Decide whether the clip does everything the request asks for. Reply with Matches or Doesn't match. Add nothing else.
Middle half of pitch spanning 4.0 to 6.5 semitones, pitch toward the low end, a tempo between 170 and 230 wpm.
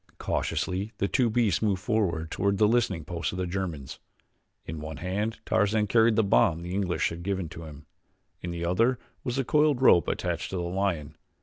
Matches